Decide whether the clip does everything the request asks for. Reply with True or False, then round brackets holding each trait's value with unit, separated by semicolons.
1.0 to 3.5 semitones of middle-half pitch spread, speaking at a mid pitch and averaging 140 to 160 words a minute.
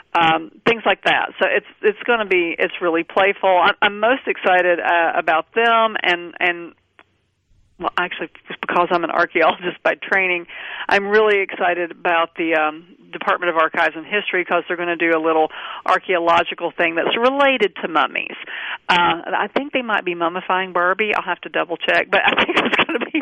False (3.1 semitones; 180 Hz; 190 wpm)